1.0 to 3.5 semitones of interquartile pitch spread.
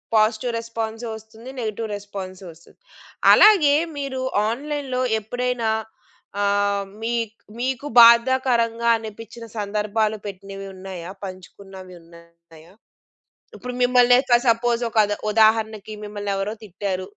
Yes: average, 3.1 semitones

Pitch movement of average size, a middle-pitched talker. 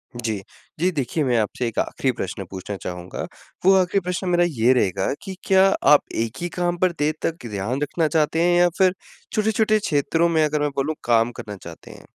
No: wide, 7.3 semitones; medium, 150 Hz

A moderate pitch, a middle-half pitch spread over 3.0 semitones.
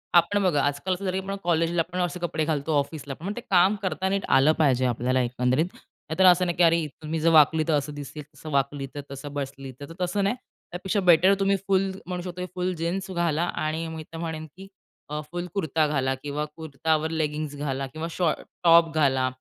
Yes: medium, 160 Hz; average, 3.7 semitones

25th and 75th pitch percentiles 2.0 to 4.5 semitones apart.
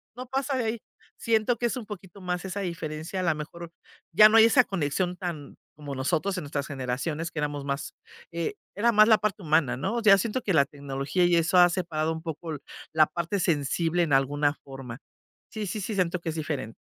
No: average, 5.1 semitones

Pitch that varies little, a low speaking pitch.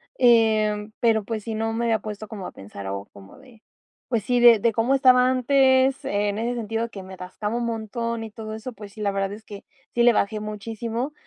No: narrow, 2.3 semitones; high, 225 Hz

